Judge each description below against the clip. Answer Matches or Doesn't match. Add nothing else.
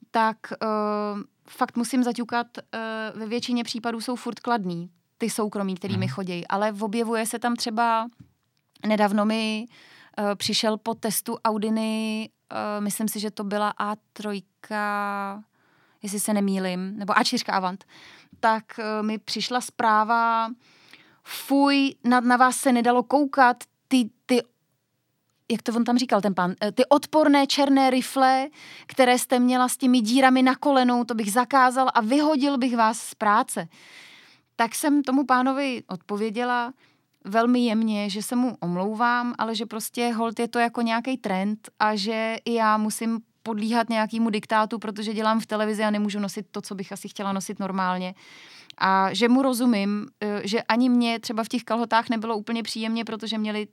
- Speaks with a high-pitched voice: Matches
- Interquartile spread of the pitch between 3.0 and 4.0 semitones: Doesn't match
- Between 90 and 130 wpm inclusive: Doesn't match